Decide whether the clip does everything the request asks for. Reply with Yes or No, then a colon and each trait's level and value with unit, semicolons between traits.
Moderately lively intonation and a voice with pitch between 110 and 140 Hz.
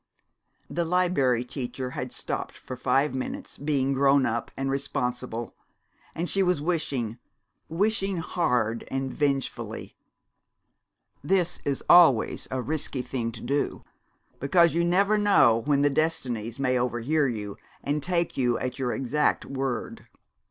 Yes: average, 4.7 semitones; low, 135 Hz